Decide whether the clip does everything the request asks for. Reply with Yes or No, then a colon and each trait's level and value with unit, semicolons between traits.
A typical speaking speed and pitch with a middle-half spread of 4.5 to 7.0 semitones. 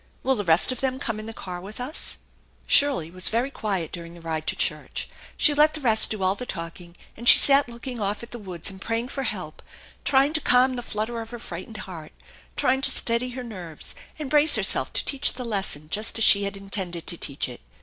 No: fast, 240 wpm; wide, 5.6 semitones